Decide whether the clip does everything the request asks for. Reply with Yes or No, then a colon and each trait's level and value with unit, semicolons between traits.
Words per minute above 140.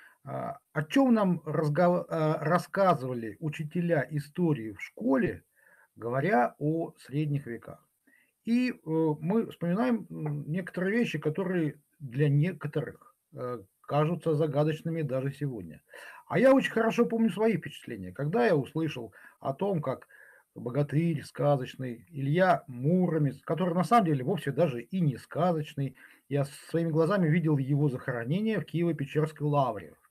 No: average, 120 wpm